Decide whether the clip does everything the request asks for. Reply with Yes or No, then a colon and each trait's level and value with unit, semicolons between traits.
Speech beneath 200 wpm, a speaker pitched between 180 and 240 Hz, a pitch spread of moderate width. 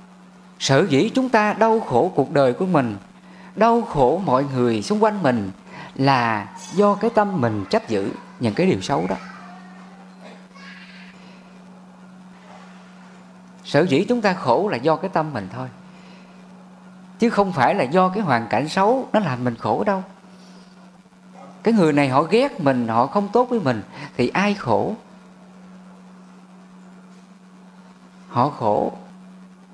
Yes: average, 140 wpm; medium, 185 Hz; average, 3.8 semitones